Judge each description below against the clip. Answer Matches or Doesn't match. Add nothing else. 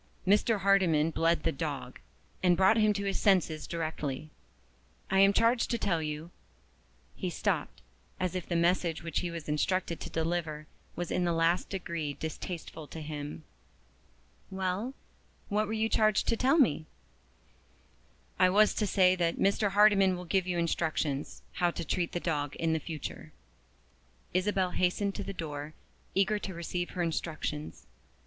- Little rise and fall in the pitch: Doesn't match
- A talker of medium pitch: Matches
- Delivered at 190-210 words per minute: Doesn't match